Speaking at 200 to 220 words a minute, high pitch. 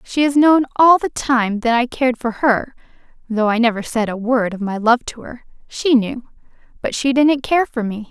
Yes: fast, 205 wpm; high, 245 Hz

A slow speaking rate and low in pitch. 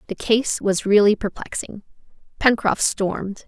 No: slow, 120 wpm; high, 210 Hz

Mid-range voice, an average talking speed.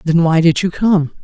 No: medium, 170 Hz; fast, 245 wpm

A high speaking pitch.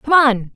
Yes: very high, 250 Hz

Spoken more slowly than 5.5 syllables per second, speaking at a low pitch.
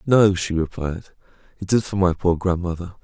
Yes: 4.9 syllables/s; very low, 90 Hz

